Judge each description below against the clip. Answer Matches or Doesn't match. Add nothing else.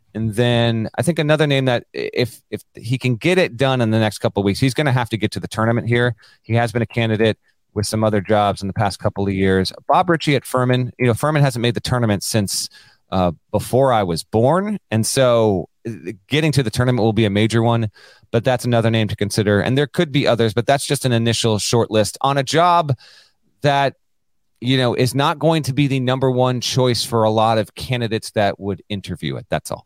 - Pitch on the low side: Matches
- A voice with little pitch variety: Doesn't match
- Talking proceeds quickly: Matches